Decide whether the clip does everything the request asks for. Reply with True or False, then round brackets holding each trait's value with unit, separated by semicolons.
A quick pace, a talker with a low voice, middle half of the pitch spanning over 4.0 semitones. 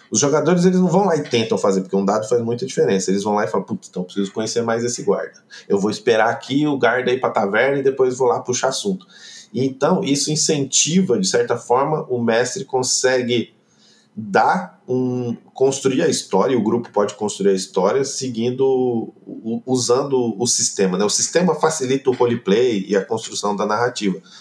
False (195 wpm; 125 Hz; 3.4 semitones)